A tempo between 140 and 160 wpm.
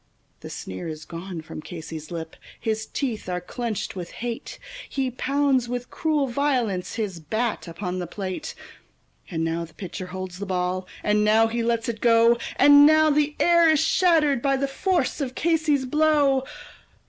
No: average, 170 wpm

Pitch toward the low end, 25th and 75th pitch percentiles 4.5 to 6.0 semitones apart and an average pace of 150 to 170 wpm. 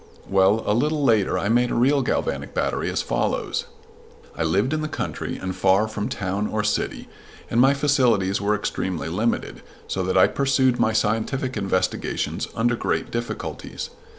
Yes: low, 110 Hz; average, 5.0 semitones; average, 165 wpm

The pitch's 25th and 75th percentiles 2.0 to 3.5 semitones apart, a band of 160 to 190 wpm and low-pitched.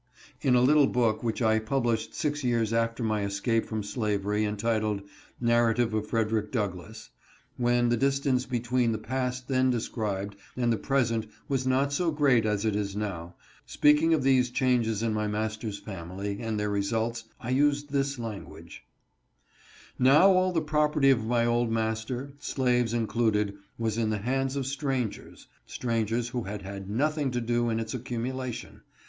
Yes: average, 3.2 semitones; average, 170 wpm; low, 115 Hz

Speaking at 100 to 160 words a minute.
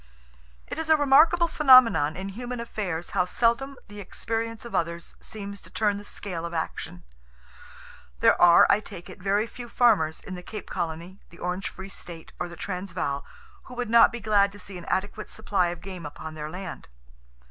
No: average, 190 wpm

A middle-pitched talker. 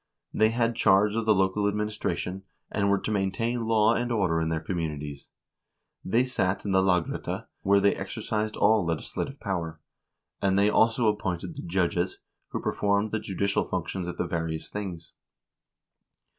No: low, 100 Hz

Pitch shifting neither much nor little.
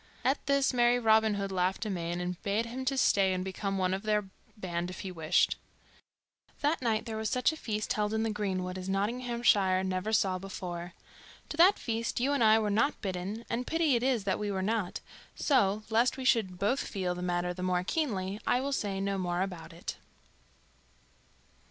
Yes: average, 4.1 semitones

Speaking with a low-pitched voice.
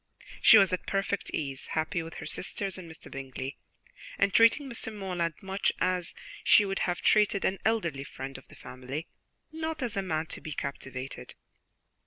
No: medium, 185 Hz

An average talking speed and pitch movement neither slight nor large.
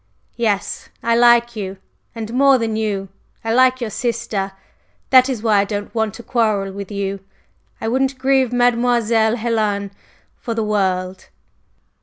Yes: average, 150 wpm; average, 3.0 semitones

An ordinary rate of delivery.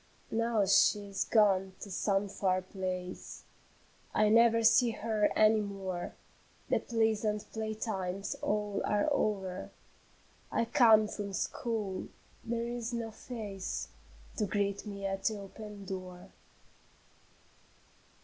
No: slow, 120 wpm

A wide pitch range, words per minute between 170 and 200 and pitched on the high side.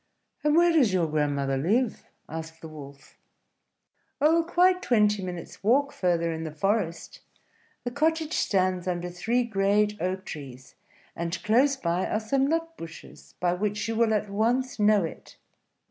No: wide, 6.7 semitones; average, 155 wpm; high, 205 Hz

